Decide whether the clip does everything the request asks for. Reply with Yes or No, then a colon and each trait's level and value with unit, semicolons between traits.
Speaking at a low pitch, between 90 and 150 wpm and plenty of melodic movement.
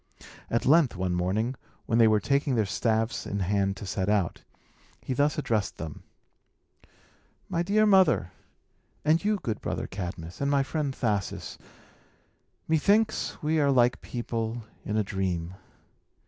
Yes: low, 115 Hz; average, 145 wpm; wide, 6.7 semitones